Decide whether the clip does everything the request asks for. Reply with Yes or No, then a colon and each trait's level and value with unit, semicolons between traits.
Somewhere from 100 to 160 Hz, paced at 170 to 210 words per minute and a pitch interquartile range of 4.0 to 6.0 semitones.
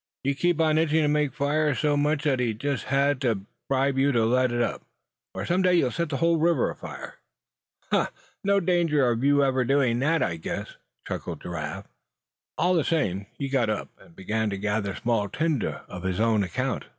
Yes: low, 135 Hz; average, 195 wpm; average, 5.2 semitones